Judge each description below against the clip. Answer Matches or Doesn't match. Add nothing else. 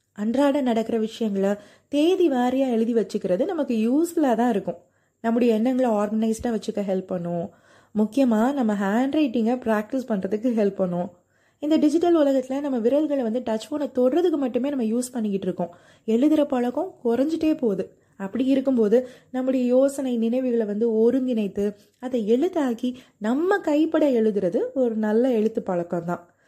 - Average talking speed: Doesn't match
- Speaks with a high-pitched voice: Matches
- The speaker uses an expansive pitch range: Doesn't match